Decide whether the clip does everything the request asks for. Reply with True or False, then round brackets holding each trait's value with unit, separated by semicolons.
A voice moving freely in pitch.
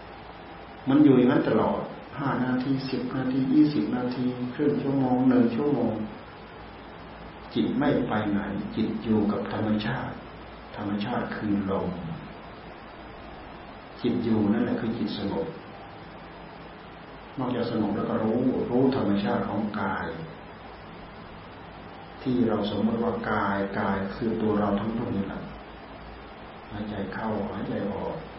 False (3.7 semitones)